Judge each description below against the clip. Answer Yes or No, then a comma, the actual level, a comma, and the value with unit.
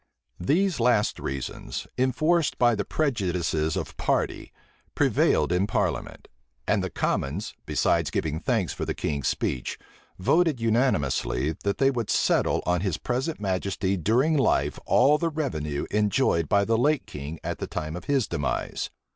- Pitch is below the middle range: Yes, low, 105 Hz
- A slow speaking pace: No, average, 150 wpm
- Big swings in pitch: Yes, wide, 8.6 semitones